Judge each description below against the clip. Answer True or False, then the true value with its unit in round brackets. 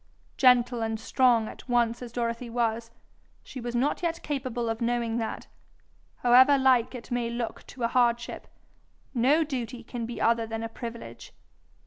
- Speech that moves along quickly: False (160 wpm)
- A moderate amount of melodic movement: False (1.5 semitones)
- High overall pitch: True (240 Hz)